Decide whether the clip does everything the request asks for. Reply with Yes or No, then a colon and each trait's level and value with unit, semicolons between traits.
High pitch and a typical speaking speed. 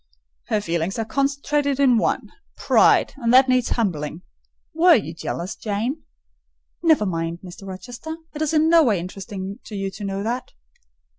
Yes: high, 225 Hz; average, 155 wpm